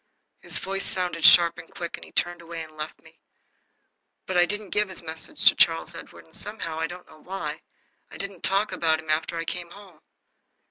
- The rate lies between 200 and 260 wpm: Yes, fast, 205 wpm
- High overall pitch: No, medium, 170 Hz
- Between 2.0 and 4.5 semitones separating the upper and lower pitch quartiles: Yes, narrow, 2.6 semitones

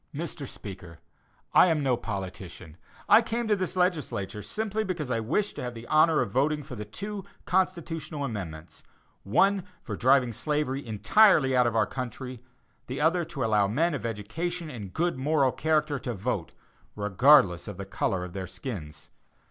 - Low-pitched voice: Yes, low, 130 Hz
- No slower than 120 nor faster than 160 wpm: No, average, 170 wpm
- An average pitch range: No, wide, 7.7 semitones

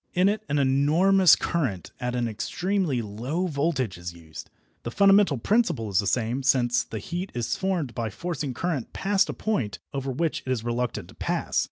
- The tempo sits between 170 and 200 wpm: Yes, average, 185 wpm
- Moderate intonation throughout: No, wide, 7.2 semitones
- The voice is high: No, low, 135 Hz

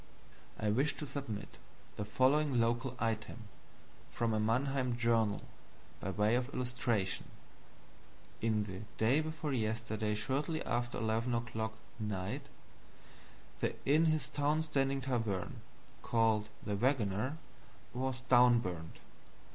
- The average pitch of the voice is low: Yes, low, 120 Hz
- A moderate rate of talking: No, slow, 85 wpm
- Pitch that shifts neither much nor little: Yes, average, 3.7 semitones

